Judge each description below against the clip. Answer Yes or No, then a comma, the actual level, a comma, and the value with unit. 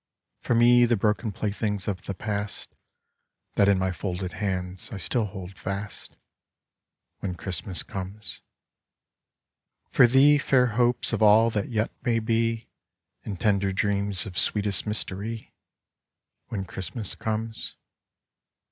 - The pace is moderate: No, slow, 125 wpm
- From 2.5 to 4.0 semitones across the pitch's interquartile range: Yes, average, 2.9 semitones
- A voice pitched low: Yes, low, 105 Hz